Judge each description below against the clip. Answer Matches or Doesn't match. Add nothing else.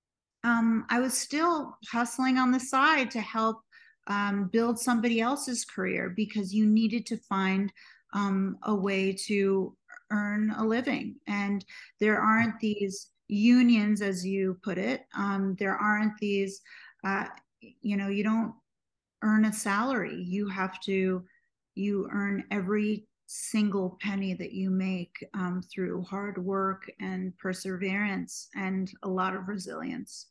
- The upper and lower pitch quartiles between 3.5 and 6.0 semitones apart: Doesn't match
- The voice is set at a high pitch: Matches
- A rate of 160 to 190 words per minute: Doesn't match